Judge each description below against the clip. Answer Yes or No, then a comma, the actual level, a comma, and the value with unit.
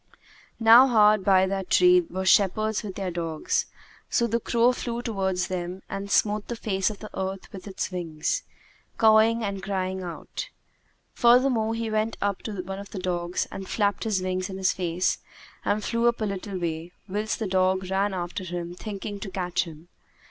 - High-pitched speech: Yes, high, 195 Hz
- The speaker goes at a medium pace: Yes, average, 185 wpm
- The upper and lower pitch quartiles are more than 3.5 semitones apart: No, average, 2.8 semitones